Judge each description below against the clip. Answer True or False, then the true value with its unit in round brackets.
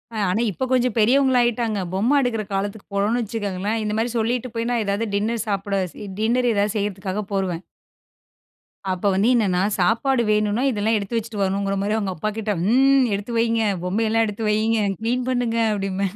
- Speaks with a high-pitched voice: True (215 Hz)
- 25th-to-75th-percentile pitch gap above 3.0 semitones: False (2.6 semitones)